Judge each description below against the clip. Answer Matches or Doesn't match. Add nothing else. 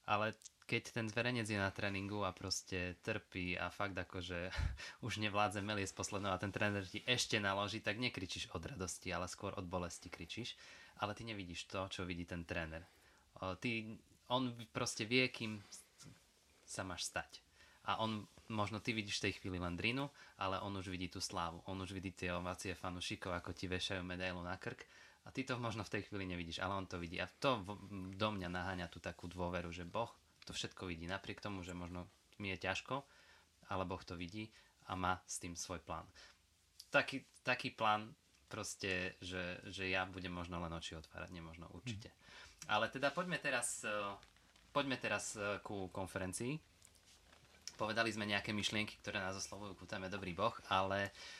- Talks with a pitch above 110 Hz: Doesn't match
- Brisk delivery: Matches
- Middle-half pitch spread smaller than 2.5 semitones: Doesn't match